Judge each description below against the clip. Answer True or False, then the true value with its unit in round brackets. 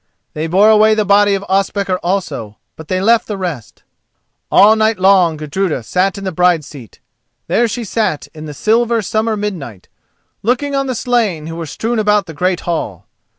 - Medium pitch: False (195 Hz)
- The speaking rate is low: False (185 wpm)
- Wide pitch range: False (4.9 semitones)